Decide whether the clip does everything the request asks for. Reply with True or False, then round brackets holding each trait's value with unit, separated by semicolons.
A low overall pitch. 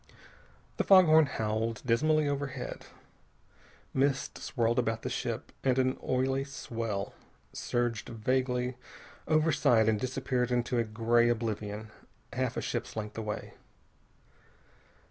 True (120 Hz)